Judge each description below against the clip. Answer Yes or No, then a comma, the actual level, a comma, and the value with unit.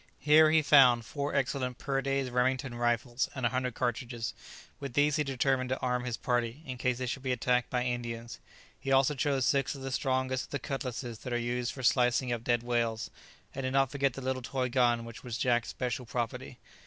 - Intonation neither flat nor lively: No, narrow, 1.9 semitones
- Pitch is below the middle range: Yes, low, 125 Hz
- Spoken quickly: Yes, fast, 210 wpm